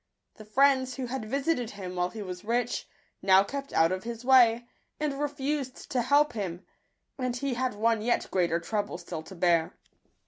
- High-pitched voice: Yes, high, 235 Hz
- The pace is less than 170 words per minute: No, average, 185 wpm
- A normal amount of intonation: No, wide, 5.8 semitones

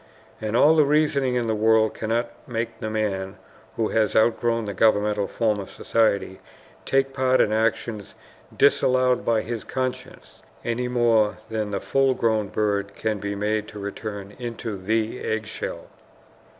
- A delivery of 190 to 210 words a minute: No, average, 155 wpm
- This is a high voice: No, low, 110 Hz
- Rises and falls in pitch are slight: Yes, narrow, 2.3 semitones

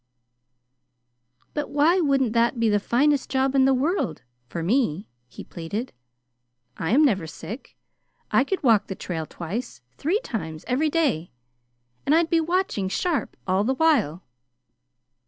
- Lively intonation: Yes, wide, 7.6 semitones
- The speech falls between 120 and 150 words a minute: Yes, average, 145 wpm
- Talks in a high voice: Yes, very high, 250 Hz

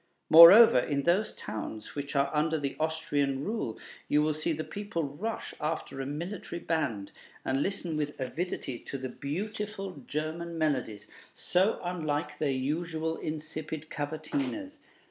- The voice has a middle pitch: Yes, medium, 155 Hz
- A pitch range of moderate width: Yes, average, 3.4 semitones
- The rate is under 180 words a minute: Yes, average, 140 wpm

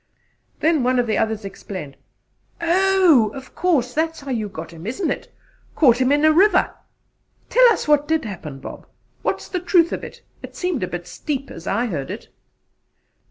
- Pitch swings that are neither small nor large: No, wide, 7.6 semitones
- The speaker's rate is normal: Yes, average, 190 wpm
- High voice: Yes, very high, 275 Hz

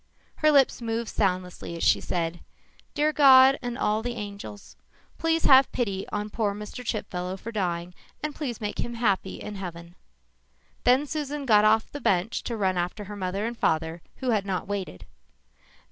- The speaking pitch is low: No, high, 210 Hz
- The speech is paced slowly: No, average, 175 wpm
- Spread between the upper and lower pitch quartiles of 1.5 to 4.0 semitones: No, average, 4.9 semitones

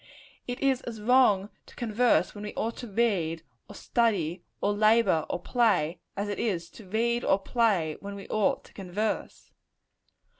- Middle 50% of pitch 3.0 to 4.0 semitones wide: Yes, average, 3.7 semitones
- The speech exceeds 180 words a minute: No, average, 165 wpm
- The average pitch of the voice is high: Yes, high, 210 Hz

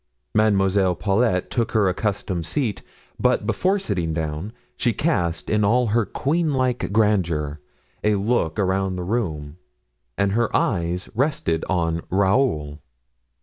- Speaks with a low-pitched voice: Yes, low, 100 Hz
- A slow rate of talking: Yes, slow, 130 wpm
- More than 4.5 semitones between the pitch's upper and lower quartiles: Yes, average, 5.2 semitones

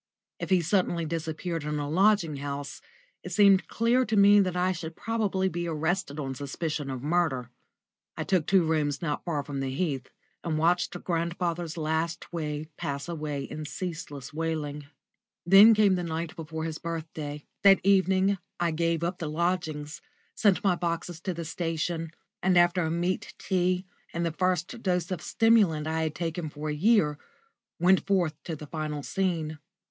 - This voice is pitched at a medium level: Yes, medium, 165 Hz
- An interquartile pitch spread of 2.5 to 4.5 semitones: Yes, average, 3.1 semitones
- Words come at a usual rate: Yes, average, 170 wpm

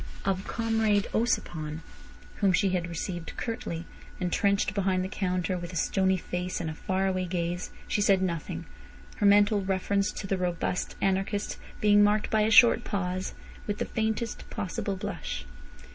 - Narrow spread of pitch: Yes, narrow, 2.3 semitones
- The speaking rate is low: No, average, 155 wpm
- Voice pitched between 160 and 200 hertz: Yes, high, 190 Hz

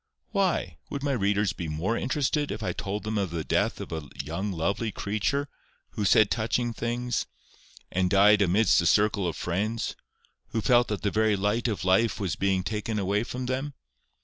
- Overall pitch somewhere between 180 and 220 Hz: No, low, 105 Hz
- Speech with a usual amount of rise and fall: Yes, average, 3.5 semitones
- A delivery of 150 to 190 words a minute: Yes, average, 185 wpm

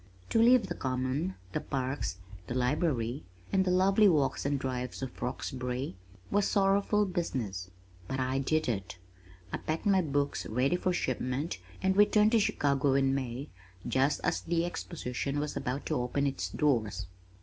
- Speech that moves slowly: No, average, 160 wpm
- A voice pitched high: No, medium, 140 Hz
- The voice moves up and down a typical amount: No, wide, 5.8 semitones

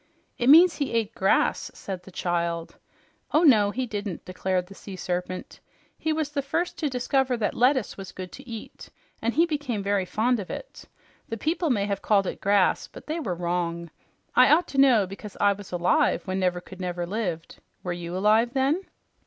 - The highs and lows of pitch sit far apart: Yes, wide, 6.5 semitones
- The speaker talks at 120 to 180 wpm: No, average, 190 wpm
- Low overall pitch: No, high, 205 Hz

